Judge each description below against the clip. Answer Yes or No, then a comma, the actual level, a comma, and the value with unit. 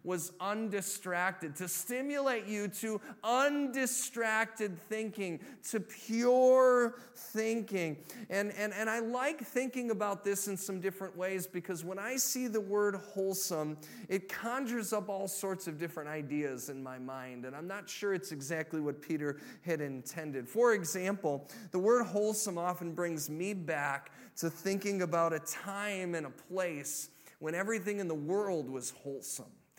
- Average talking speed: Yes, average, 150 wpm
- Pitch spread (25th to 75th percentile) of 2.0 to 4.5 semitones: No, average, 5.0 semitones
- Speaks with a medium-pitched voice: No, high, 195 Hz